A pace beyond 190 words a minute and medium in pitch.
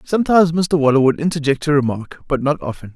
Yes: fast, 205 wpm; medium, 150 Hz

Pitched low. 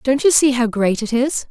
No: very high, 255 Hz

